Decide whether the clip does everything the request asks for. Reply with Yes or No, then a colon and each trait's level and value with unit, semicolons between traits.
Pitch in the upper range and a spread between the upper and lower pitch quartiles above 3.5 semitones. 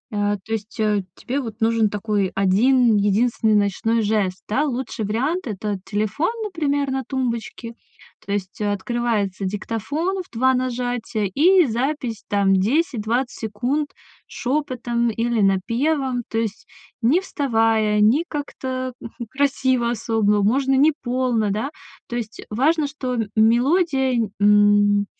Yes: high, 235 Hz; average, 4.0 semitones